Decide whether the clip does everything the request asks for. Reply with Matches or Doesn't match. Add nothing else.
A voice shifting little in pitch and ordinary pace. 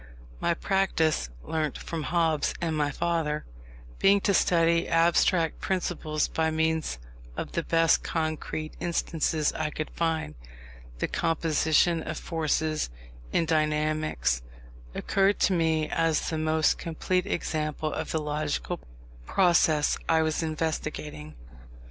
Doesn't match